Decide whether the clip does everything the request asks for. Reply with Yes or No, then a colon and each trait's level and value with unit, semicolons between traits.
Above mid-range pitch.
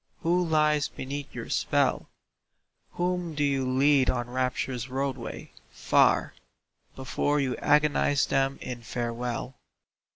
No: low, 135 Hz